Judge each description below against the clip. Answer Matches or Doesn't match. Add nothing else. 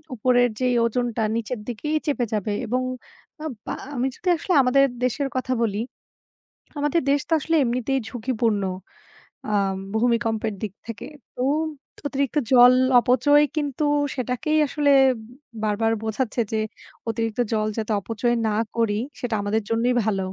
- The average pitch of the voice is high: Matches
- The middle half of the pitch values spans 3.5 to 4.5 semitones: Doesn't match